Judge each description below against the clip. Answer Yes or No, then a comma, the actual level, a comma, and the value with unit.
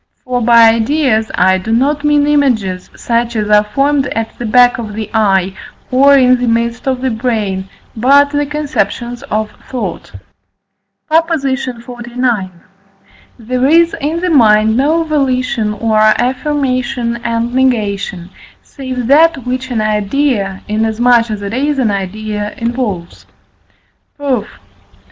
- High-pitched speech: Yes, high, 240 Hz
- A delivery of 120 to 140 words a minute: Yes, slow, 135 wpm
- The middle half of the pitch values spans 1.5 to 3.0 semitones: No, average, 3.9 semitones